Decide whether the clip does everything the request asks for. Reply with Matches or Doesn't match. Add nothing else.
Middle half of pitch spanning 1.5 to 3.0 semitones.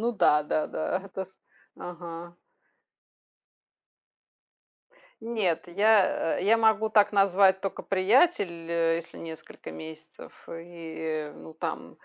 Doesn't match